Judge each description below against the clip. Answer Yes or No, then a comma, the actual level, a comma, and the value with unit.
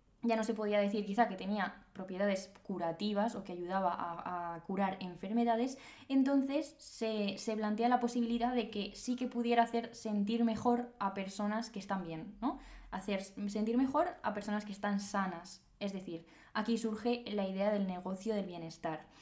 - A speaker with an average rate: Yes, average, 170 wpm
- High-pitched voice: Yes, high, 210 Hz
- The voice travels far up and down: No, average, 3.4 semitones